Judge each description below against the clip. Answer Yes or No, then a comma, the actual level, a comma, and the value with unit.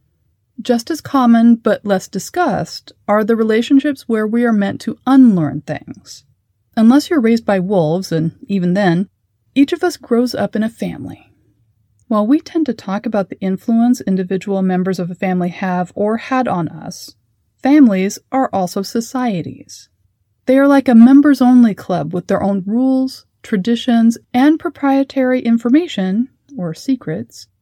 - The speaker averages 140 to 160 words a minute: Yes, average, 155 wpm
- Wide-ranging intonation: Yes, wide, 5.9 semitones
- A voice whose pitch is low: No, high, 220 Hz